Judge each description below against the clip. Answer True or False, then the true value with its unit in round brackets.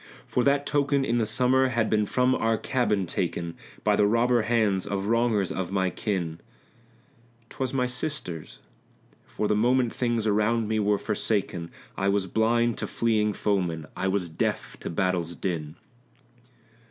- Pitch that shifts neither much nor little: True (4.0 semitones)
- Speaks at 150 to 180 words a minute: True (155 wpm)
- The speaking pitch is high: False (105 Hz)